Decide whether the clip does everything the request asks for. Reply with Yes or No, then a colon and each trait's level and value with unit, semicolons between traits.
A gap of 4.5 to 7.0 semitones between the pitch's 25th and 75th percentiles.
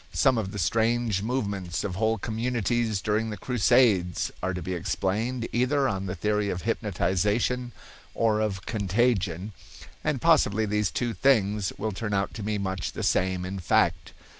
No: average, 3.5 semitones